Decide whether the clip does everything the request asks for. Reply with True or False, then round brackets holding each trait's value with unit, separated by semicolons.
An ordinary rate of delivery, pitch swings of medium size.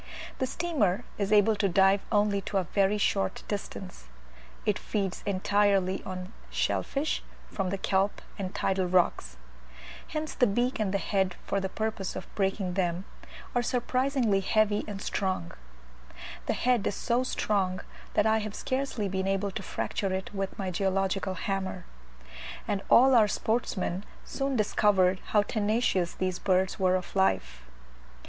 False (150 wpm; 2.3 semitones)